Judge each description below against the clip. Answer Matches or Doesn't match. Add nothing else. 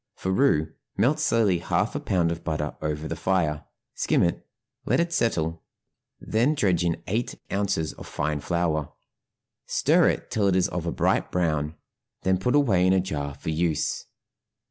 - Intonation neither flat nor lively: Matches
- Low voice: Matches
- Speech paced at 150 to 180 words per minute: Matches